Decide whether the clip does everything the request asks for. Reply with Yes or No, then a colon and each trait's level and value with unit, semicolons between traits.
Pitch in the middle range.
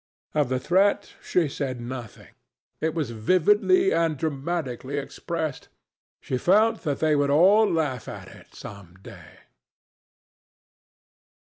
Yes: medium, 150 Hz